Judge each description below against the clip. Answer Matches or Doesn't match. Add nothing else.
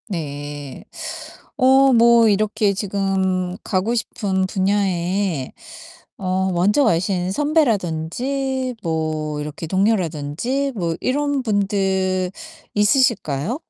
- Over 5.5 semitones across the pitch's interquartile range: Doesn't match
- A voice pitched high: Matches